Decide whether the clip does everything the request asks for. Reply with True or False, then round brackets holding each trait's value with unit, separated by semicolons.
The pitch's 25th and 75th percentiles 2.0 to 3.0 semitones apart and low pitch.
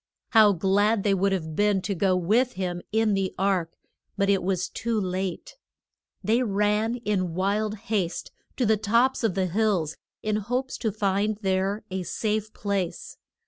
False (2.4 semitones; 200 Hz)